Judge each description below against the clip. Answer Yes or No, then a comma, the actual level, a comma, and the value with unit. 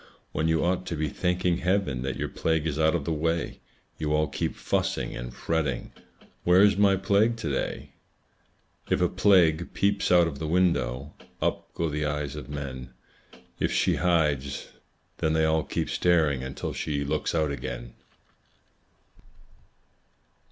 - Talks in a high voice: No, very low, 80 Hz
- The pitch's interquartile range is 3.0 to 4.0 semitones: Yes, average, 3.7 semitones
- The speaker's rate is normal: Yes, average, 160 wpm